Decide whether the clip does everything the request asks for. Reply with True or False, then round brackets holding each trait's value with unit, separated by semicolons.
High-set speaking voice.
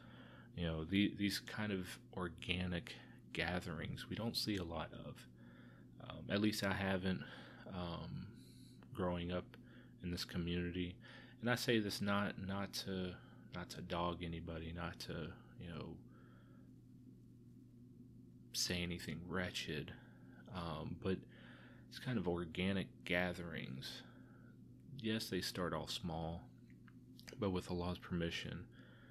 False (90 Hz)